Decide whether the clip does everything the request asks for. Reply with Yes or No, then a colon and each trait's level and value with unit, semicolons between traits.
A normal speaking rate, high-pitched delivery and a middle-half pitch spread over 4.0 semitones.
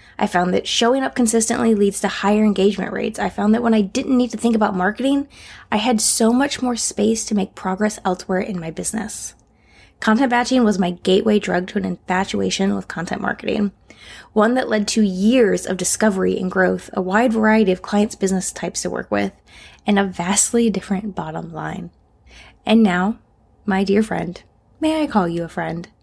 No: average, 190 wpm; high, 205 Hz; average, 3.3 semitones